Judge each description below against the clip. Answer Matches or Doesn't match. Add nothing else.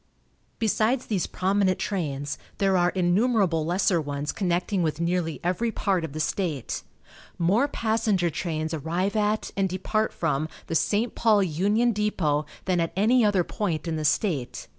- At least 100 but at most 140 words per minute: Doesn't match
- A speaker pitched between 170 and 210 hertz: Matches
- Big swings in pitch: Doesn't match